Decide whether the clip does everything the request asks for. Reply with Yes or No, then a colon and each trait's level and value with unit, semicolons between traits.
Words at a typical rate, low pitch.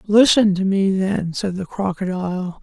No: average, 160 wpm; high, 190 Hz